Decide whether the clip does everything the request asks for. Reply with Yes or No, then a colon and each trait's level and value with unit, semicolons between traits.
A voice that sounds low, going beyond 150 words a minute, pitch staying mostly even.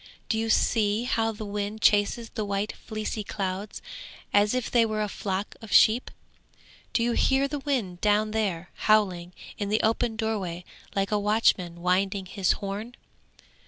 No: high, 210 Hz; average, 160 wpm; narrow, 2.1 semitones